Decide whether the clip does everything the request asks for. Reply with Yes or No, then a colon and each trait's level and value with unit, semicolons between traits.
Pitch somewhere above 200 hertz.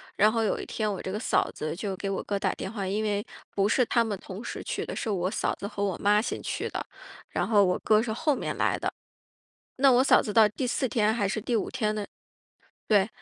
Yes: high, 210 Hz